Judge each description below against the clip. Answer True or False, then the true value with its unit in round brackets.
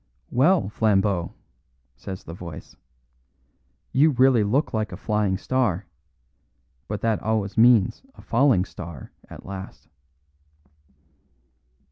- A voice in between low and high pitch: False (105 Hz)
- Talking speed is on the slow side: True (105 wpm)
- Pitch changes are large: False (4.4 semitones)